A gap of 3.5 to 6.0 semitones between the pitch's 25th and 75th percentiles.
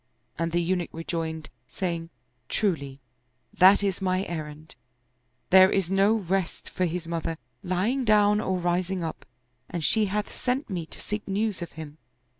No: average, 3.1 semitones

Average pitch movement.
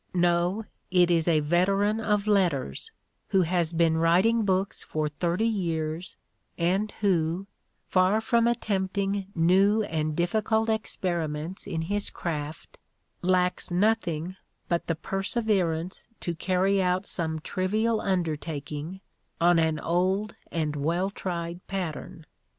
Yes: average, 3.3 semitones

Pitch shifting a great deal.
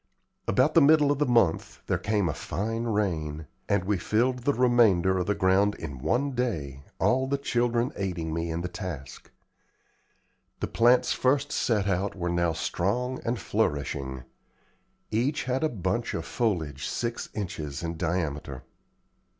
Yes: wide, 6.6 semitones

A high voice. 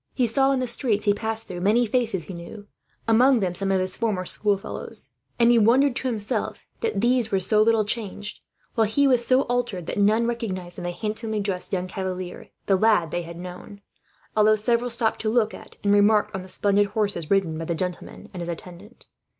Yes: high, 210 Hz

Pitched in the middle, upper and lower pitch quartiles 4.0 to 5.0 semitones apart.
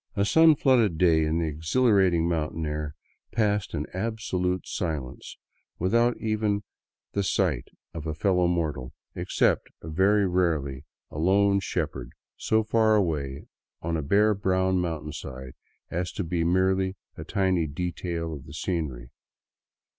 No: very low, 90 Hz; average, 4.3 semitones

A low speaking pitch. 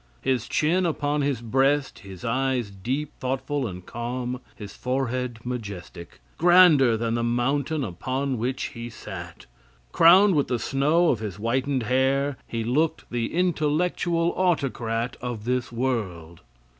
Yes: low, 130 Hz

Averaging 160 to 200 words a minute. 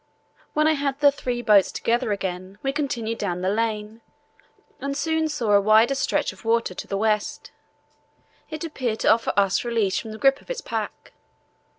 Yes: average, 185 wpm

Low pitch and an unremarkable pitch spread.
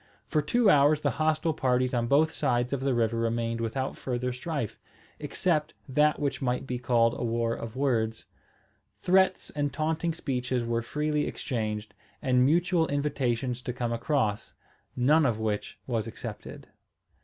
Yes: low, 125 Hz; average, 4.2 semitones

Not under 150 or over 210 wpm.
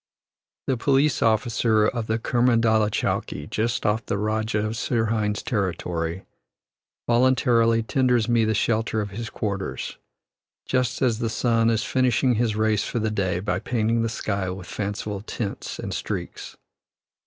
No: average, 140 wpm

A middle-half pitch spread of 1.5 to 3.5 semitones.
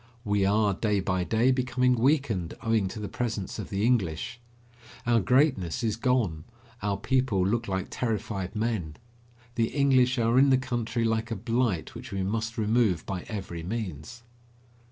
No: average, 4.0 semitones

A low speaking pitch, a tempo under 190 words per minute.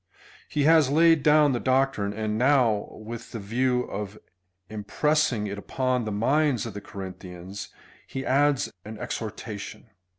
Yes: low, 120 Hz; average, 145 wpm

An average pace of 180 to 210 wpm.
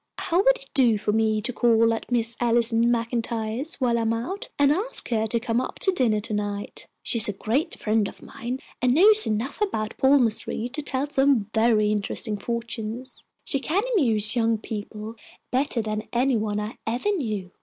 Yes: average, 190 wpm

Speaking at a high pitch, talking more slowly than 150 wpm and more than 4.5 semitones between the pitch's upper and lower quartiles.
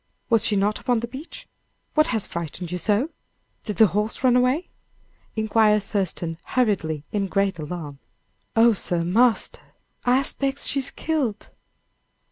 Yes: high, 215 Hz; average, 140 wpm; average, 5.0 semitones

